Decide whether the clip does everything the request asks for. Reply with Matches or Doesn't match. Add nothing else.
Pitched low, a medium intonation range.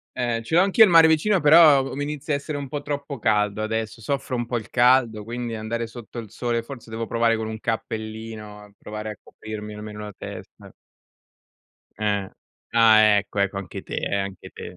Matches